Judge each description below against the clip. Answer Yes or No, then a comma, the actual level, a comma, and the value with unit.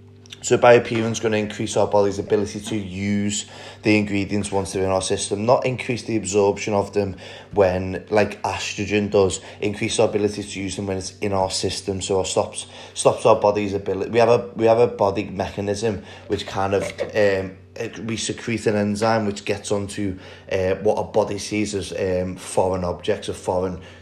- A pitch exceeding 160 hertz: No, low, 100 Hz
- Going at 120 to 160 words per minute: No, average, 190 wpm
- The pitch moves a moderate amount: No, narrow, 1.9 semitones